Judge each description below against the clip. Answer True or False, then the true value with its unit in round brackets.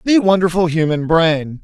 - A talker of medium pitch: True (170 Hz)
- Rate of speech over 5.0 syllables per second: False (4.6 syllables/s)